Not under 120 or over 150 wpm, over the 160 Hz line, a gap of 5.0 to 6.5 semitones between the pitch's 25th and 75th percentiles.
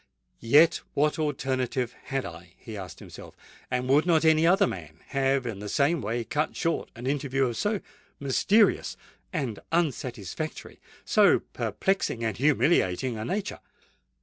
No: average, 140 wpm; low, 135 Hz; average, 5.3 semitones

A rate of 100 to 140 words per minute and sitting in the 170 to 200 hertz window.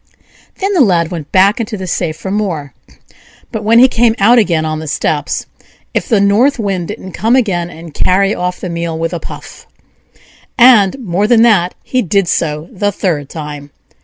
No: average, 190 wpm; high, 190 Hz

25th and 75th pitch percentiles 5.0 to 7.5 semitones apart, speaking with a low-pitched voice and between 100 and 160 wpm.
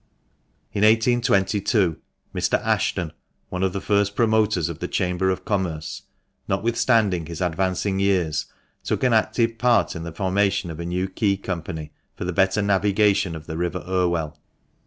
No: average, 3.1 semitones; very low, 95 Hz; average, 155 wpm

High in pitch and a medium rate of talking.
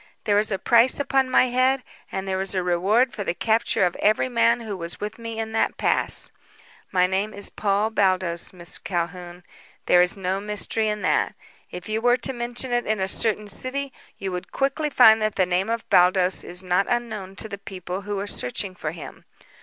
No: high, 205 Hz; fast, 210 wpm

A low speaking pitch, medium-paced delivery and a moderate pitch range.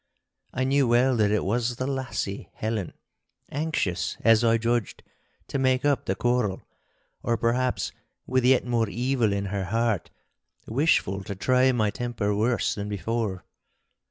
Yes: low, 115 Hz; average, 150 wpm; average, 3.6 semitones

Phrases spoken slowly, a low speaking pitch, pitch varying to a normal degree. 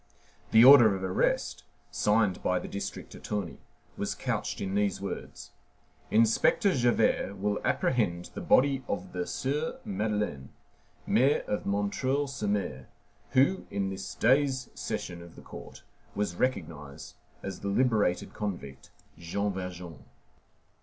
Yes: slow, 130 wpm; low, 100 Hz; average, 4.9 semitones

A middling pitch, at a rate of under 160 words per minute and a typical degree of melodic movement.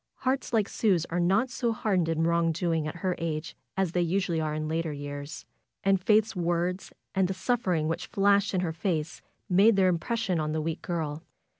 No: medium, 175 Hz; average, 195 wpm; average, 3.3 semitones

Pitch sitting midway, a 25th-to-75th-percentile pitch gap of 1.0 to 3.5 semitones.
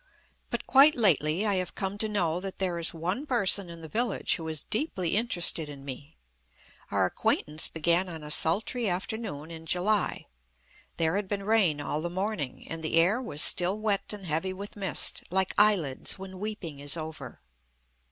No: medium, 180 Hz; average, 4.3 semitones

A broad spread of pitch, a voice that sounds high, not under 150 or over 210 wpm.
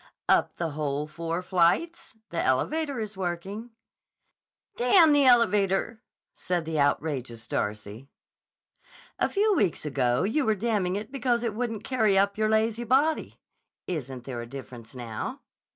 No: wide, 8.6 semitones; high, 195 Hz; average, 140 wpm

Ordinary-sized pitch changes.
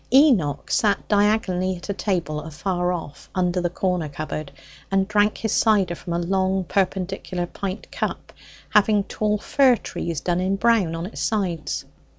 Yes: average, 3.0 semitones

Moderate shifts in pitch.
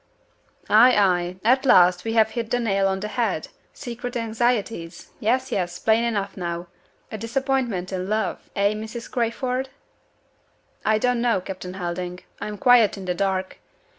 Yes: average, 4.1 semitones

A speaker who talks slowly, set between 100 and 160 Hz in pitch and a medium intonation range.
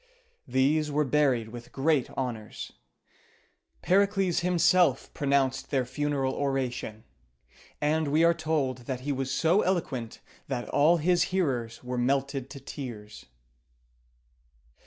Yes: slow, 115 wpm; medium, 140 Hz; average, 3.8 semitones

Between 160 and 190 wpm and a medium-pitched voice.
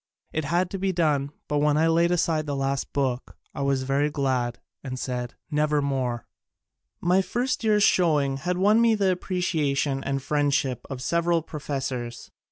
Yes: average, 175 wpm; medium, 145 Hz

